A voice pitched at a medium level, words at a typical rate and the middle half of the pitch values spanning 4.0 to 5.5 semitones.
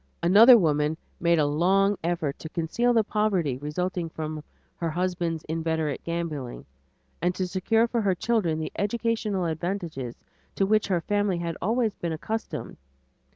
Yes: medium, 175 Hz; average, 150 wpm; average, 4.3 semitones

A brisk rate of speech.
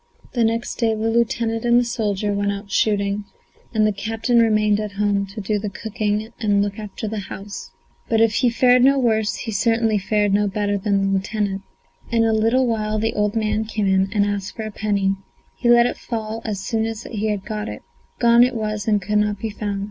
Yes: fast, 215 wpm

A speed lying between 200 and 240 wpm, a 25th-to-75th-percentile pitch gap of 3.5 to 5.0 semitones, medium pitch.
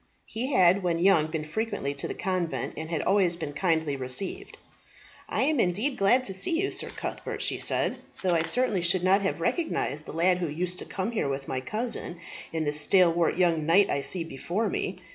Yes: fast, 205 wpm; average, 3.8 semitones; medium, 180 Hz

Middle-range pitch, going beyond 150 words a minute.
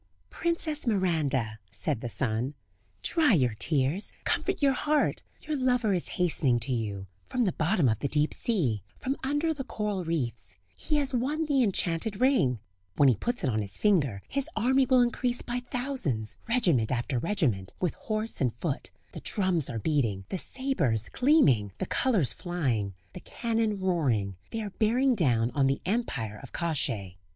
Yes: medium, 175 Hz; average, 170 wpm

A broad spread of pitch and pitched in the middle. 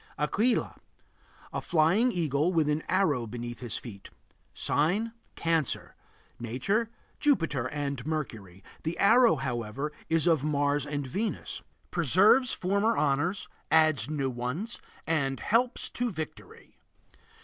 Yes: wide, 6.0 semitones; medium, 155 Hz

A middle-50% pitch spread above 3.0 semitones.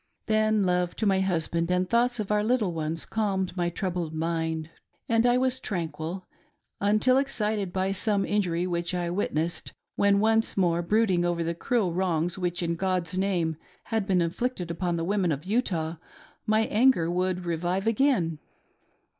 Yes: average, 3.8 semitones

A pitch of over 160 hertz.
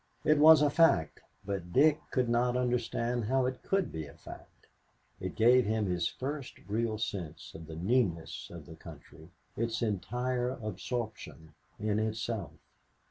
No: low, 115 Hz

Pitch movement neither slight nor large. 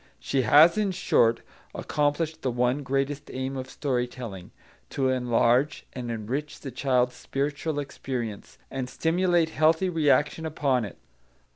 Yes: average, 3.5 semitones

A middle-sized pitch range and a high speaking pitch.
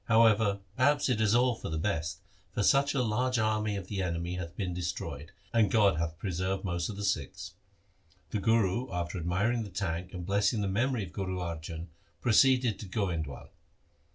No: average, 4.3 semitones; low, 100 Hz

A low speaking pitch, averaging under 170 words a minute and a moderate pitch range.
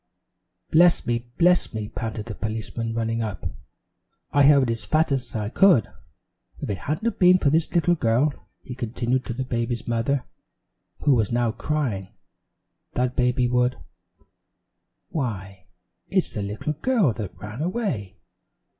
Yes: low, 120 Hz; average, 145 wpm; average, 5.0 semitones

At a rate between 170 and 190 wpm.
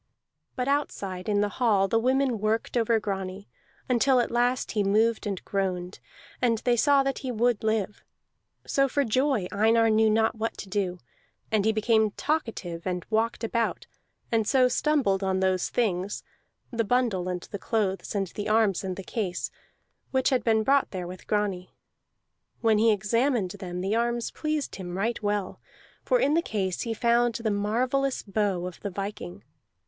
Yes: average, 175 wpm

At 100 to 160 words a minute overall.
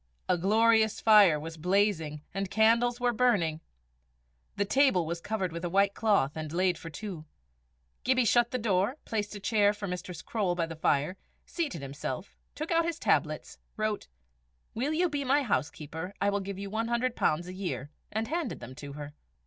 No: average, 180 wpm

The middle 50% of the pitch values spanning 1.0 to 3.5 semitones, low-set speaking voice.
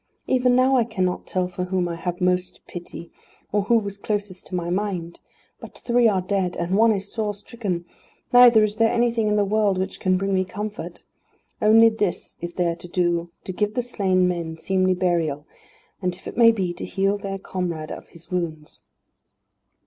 No: average, 3.1 semitones; high, 190 Hz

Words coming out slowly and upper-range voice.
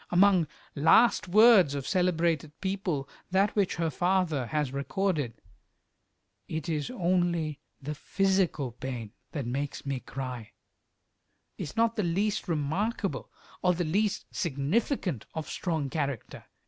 No: slow, 120 wpm; medium, 165 Hz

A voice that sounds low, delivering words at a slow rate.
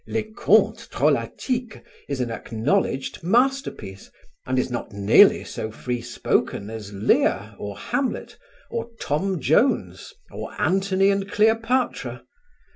No: high, 190 Hz; slow, 120 wpm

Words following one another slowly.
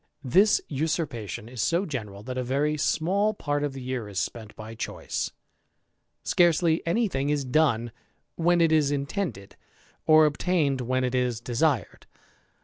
No: average, 150 wpm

